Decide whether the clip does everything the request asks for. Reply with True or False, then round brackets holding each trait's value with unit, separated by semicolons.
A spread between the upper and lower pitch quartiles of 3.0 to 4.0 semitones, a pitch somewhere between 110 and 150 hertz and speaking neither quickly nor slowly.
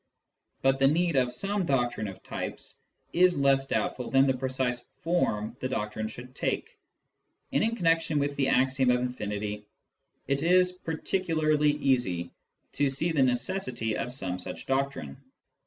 False (4.4 semitones; 135 Hz; 150 wpm)